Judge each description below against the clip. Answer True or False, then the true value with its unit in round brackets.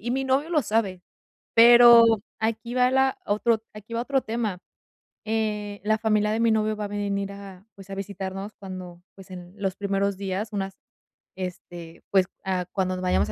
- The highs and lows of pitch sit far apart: False (2.8 semitones)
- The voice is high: True (205 Hz)